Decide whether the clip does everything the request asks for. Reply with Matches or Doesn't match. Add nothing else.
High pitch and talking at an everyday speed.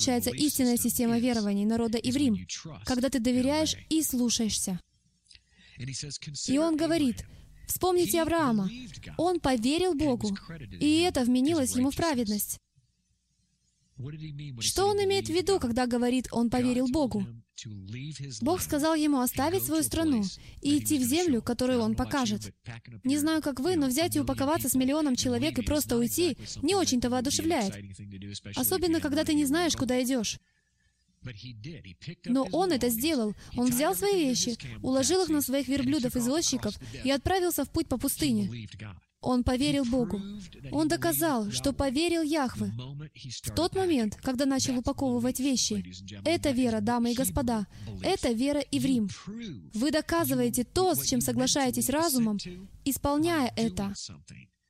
Matches